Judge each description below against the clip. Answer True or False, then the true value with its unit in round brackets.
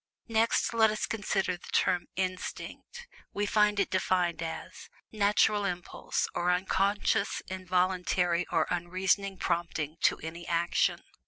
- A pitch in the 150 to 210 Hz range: True (185 Hz)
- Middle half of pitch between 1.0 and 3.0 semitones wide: True (2.6 semitones)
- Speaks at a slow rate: True (120 wpm)